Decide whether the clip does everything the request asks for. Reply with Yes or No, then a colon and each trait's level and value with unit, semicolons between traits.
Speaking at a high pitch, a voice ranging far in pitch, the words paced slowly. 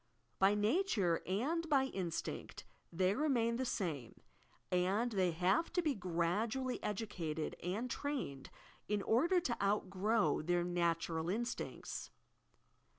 Yes: high, 200 Hz; wide, 5.7 semitones; slow, 115 wpm